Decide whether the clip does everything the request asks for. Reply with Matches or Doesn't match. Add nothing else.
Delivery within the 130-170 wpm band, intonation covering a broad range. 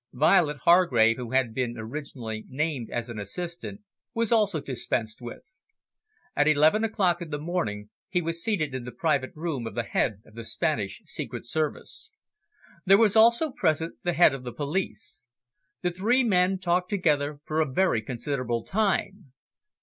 Matches